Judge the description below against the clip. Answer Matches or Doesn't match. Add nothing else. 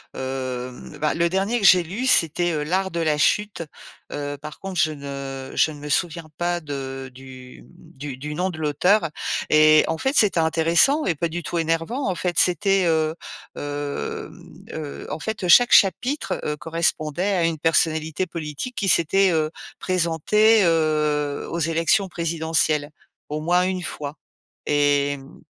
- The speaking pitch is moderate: Matches